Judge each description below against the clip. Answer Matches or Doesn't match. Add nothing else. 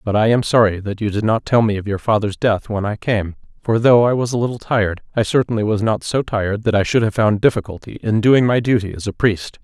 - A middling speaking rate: Doesn't match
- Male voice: Matches